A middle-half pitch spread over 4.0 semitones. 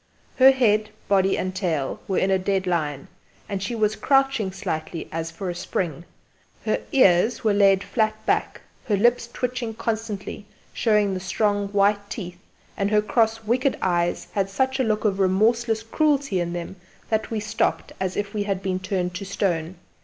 No: average, 3.1 semitones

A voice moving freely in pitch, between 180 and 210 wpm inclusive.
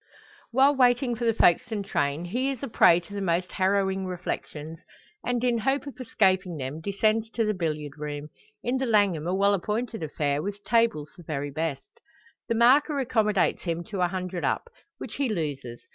Yes: wide, 6.2 semitones; average, 185 wpm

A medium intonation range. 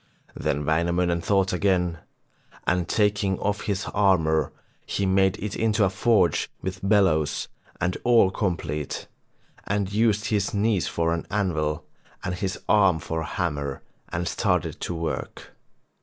Yes: average, 3.6 semitones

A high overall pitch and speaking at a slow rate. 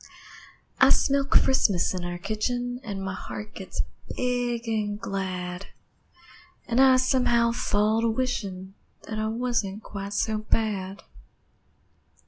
Yes: high, 215 Hz; slow, 120 wpm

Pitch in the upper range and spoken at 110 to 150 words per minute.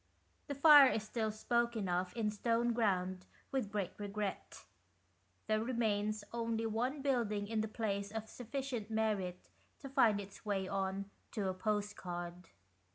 Yes: high, 215 Hz; average, 140 wpm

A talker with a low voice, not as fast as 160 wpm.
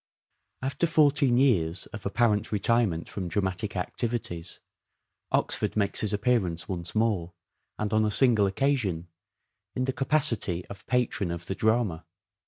Yes: low, 105 Hz; slow, 135 wpm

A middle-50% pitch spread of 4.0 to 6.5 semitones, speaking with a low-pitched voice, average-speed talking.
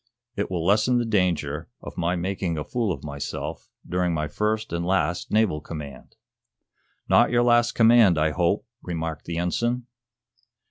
Yes: average, 5.2 semitones; very low, 90 Hz; average, 155 wpm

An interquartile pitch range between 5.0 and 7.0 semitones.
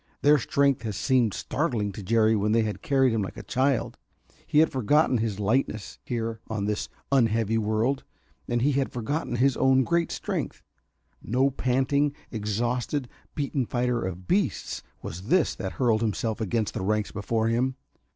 No: average, 3.7 semitones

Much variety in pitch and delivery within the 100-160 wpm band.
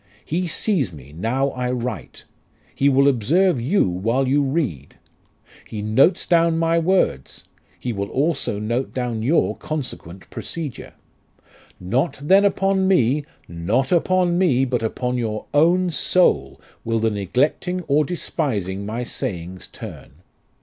Yes: wide, 7.5 semitones; slow, 135 wpm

